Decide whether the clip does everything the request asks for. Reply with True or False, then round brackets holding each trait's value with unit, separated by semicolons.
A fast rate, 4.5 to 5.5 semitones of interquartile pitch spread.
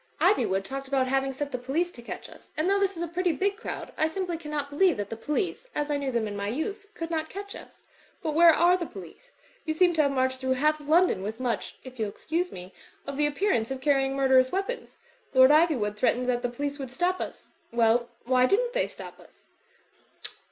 True (230 wpm; 5.2 semitones)